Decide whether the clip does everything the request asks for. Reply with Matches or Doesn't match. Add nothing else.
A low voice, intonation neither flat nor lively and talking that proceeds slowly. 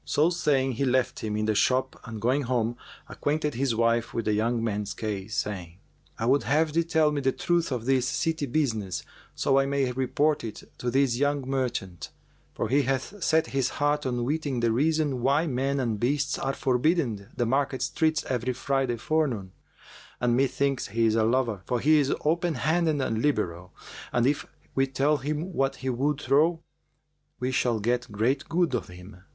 Doesn't match